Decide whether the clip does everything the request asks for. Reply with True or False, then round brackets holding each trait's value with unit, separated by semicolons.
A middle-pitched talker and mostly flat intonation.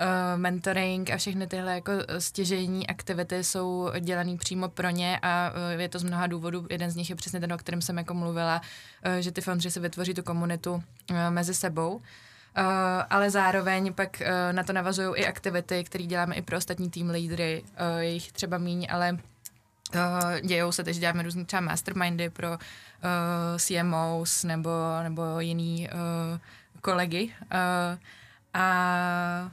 True (175 Hz; 1.2 semitones)